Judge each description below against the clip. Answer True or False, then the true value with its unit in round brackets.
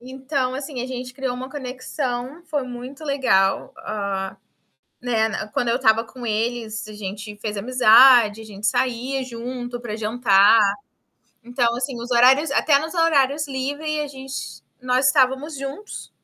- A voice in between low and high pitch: False (250 Hz)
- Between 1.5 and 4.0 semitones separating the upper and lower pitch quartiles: True (3.3 semitones)